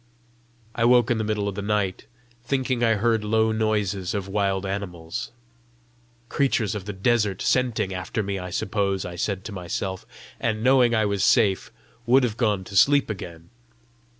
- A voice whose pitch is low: Yes, low, 105 Hz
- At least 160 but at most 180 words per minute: Yes, average, 170 wpm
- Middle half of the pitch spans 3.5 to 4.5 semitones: No, average, 3.0 semitones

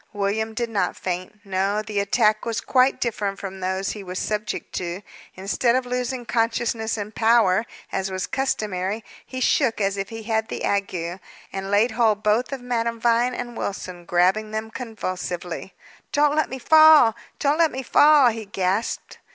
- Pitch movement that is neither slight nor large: Yes, average, 3.6 semitones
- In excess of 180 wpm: No, average, 170 wpm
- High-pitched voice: Yes, high, 215 Hz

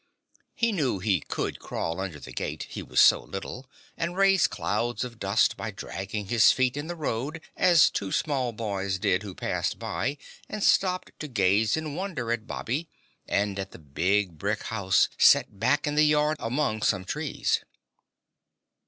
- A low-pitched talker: Yes, low, 115 Hz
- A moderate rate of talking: Yes, average, 170 wpm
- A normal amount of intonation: No, wide, 7.4 semitones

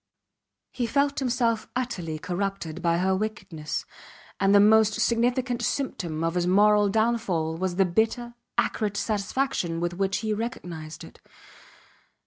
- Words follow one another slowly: Yes, slow, 130 wpm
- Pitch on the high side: Yes, high, 205 Hz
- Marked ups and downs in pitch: No, average, 4.9 semitones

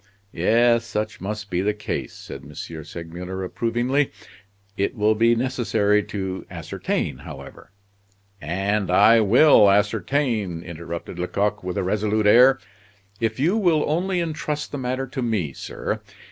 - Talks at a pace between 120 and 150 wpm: Yes, average, 140 wpm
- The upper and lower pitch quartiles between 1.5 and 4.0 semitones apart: No, average, 4.5 semitones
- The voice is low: Yes, low, 105 Hz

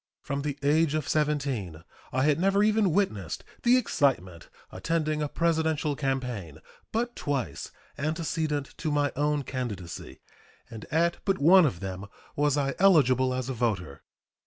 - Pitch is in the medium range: Yes, medium, 145 Hz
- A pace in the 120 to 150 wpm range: Yes, average, 145 wpm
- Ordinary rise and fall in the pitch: Yes, average, 4.3 semitones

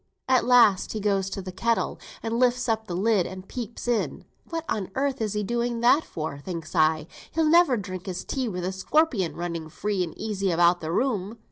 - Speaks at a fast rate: Yes, fast, 210 wpm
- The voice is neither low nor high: No, high, 210 Hz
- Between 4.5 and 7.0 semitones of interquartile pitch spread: Yes, average, 5.0 semitones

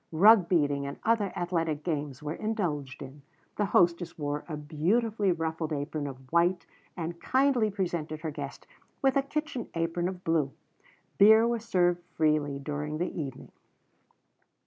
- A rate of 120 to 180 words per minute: Yes, average, 145 wpm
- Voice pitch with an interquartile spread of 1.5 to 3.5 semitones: No, average, 4.9 semitones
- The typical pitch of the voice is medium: Yes, medium, 165 Hz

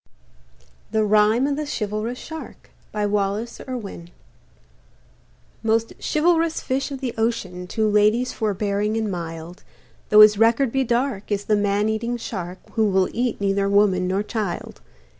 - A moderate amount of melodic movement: Yes, average, 3.0 semitones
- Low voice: No, high, 215 Hz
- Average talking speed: Yes, average, 145 wpm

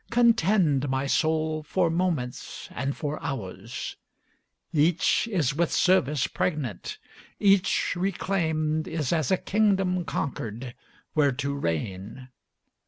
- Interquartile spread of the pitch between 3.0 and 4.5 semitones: No, wide, 5.4 semitones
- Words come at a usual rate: No, slow, 105 wpm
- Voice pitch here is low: No, medium, 155 Hz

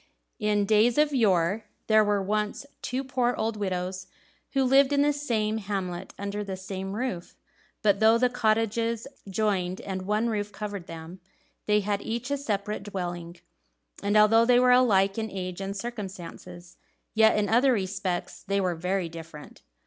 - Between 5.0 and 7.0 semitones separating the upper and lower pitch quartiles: No, average, 3.2 semitones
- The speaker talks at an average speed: Yes, average, 165 wpm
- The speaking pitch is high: Yes, high, 205 Hz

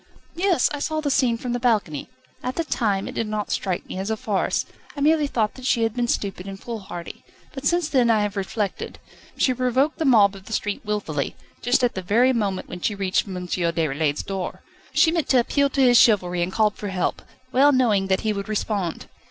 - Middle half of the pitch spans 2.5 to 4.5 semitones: No, average, 4.9 semitones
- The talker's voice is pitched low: No, high, 215 Hz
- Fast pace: Yes, fast, 220 wpm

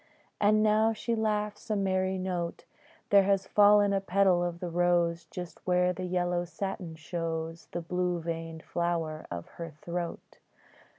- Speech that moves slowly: No, average, 155 wpm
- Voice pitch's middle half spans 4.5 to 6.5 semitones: No, average, 2.7 semitones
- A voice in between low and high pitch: Yes, medium, 180 Hz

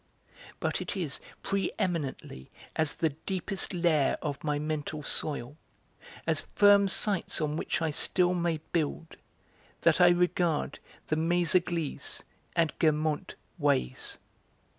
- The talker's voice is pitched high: No, medium, 160 Hz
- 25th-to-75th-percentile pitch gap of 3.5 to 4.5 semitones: No, average, 2.9 semitones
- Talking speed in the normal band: No, slow, 120 wpm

